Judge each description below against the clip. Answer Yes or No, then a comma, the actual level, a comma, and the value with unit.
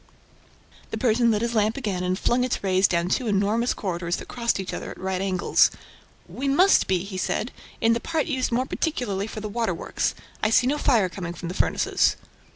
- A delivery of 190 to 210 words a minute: Yes, fast, 205 wpm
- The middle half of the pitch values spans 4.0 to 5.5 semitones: Yes, average, 4.6 semitones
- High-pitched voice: Yes, high, 215 Hz